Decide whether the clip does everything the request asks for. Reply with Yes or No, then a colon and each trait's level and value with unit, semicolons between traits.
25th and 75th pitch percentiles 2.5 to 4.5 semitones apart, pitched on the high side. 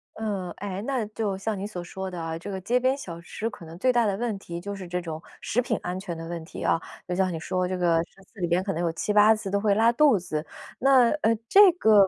Yes: average, 3.9 semitones; high, 195 Hz